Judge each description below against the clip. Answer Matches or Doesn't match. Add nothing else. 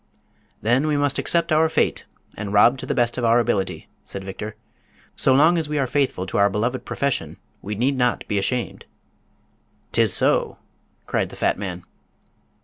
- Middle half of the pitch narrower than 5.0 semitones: Doesn't match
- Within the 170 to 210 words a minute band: Matches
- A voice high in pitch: Doesn't match